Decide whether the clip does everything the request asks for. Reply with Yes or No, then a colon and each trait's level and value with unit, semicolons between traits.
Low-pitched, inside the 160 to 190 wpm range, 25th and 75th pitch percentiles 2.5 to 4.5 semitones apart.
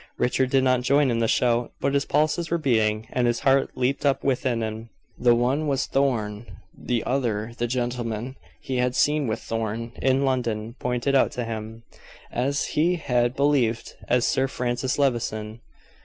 Yes: low, 125 Hz; average, 170 wpm; average, 2.9 semitones